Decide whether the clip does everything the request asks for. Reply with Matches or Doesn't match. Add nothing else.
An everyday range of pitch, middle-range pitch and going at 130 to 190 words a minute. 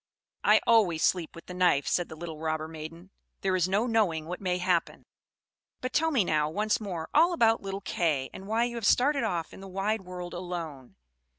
Doesn't match